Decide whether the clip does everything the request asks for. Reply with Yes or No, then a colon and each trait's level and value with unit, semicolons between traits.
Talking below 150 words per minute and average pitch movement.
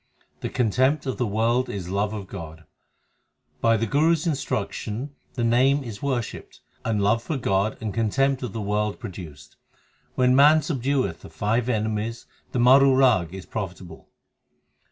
No: average, 160 wpm; average, 4.3 semitones